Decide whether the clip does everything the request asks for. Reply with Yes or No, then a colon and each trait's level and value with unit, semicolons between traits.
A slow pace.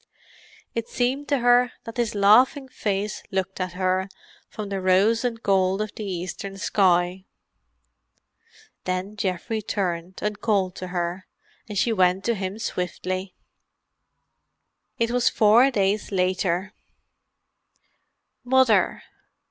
Yes: slow, 120 wpm